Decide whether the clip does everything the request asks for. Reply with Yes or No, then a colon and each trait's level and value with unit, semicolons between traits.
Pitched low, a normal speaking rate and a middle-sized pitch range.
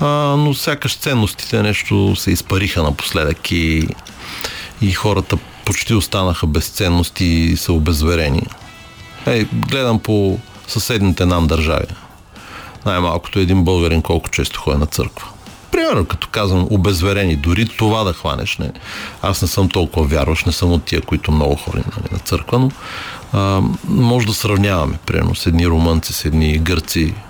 Yes: very low, 95 Hz; average, 145 wpm; average, 4.0 semitones